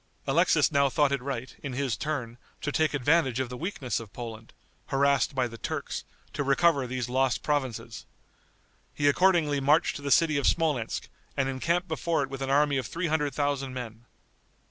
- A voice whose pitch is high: No, medium, 140 Hz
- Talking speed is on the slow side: No, average, 185 wpm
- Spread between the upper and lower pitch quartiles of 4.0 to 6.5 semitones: No, average, 2.7 semitones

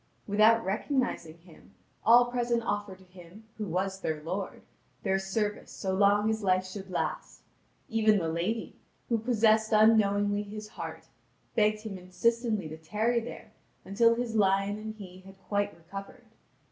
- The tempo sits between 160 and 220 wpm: No, average, 150 wpm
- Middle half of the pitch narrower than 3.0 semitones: Yes, narrow, 2.6 semitones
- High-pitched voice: Yes, high, 205 Hz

